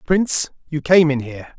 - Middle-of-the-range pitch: Yes, medium, 150 Hz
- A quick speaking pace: No, average, 190 wpm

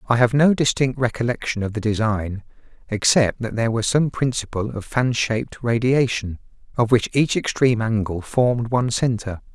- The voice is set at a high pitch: No, low, 115 Hz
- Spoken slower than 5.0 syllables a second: No, 5.2 syllables/s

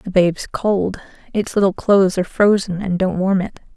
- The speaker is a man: No, female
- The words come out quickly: No, average, 190 wpm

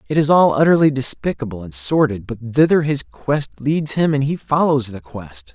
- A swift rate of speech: No, average, 195 wpm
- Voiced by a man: Yes, male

